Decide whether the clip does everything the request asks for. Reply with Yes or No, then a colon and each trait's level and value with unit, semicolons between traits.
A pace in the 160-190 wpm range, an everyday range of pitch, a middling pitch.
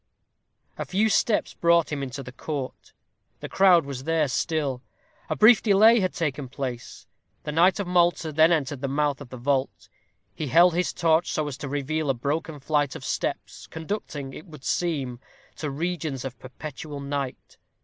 Yes: average, 175 wpm; average, 3.7 semitones; medium, 150 Hz